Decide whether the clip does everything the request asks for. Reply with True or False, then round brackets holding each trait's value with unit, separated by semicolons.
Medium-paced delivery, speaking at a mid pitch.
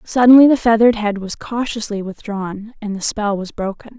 False (180 wpm; 215 Hz)